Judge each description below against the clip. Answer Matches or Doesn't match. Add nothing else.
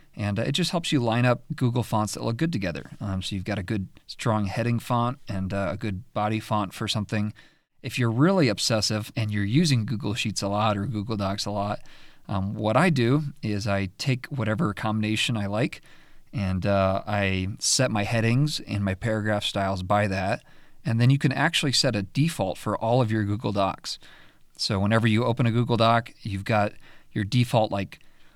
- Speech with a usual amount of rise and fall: Matches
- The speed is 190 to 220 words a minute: Matches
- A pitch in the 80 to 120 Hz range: Matches